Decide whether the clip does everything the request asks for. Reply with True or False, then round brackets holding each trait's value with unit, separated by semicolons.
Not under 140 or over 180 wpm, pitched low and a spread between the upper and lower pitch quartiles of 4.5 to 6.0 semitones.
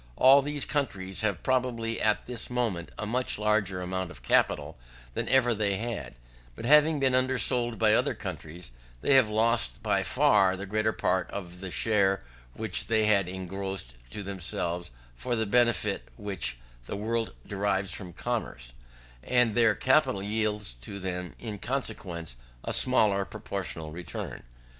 False (150 wpm; 105 Hz; 4.0 semitones)